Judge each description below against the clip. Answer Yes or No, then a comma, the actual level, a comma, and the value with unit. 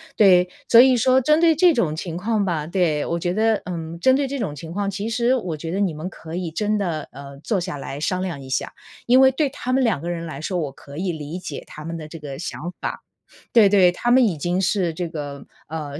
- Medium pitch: Yes, medium, 180 Hz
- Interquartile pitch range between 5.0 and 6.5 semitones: Yes, wide, 5.6 semitones